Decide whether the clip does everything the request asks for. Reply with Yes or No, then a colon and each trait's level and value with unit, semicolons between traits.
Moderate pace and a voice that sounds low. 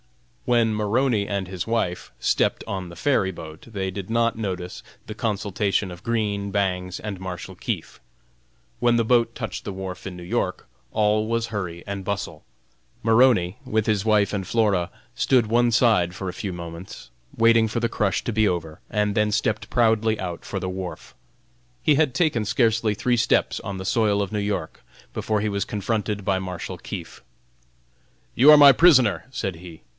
Yes: average, 180 wpm; low, 105 Hz